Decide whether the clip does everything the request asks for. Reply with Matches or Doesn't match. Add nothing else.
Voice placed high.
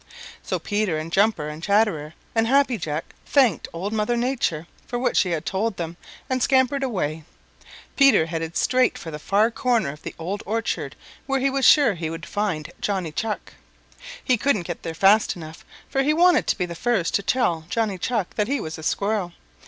Matches